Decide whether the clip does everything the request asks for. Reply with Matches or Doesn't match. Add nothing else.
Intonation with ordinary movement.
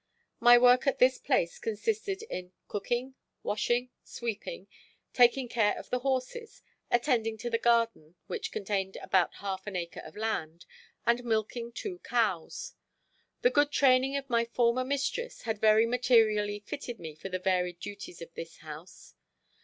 Matches